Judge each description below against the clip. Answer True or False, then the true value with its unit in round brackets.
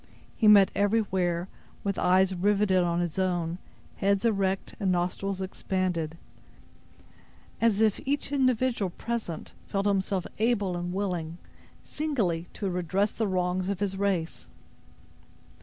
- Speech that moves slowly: True (125 wpm)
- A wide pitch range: False (2.4 semitones)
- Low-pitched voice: False (190 Hz)